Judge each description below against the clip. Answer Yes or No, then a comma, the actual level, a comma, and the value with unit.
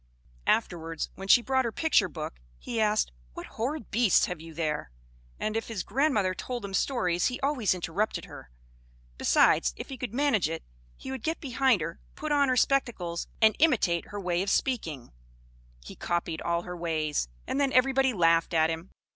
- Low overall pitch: No, high, 205 Hz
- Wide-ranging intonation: Yes, wide, 7.3 semitones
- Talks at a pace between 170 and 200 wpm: Yes, average, 180 wpm